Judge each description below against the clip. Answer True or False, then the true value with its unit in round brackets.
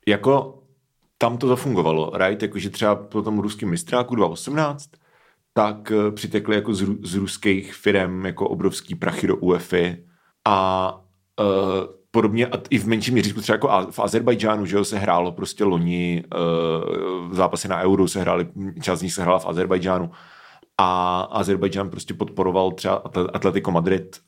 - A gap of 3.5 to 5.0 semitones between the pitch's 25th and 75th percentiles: False (2.7 semitones)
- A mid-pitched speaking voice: False (100 Hz)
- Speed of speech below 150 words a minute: False (170 wpm)